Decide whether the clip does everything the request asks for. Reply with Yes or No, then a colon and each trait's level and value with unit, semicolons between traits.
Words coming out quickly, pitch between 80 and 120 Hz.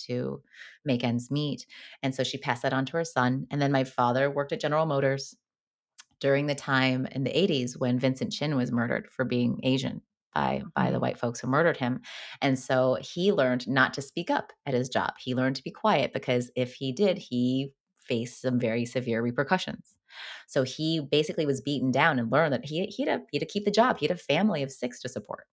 No: fast, 220 wpm; low, 135 Hz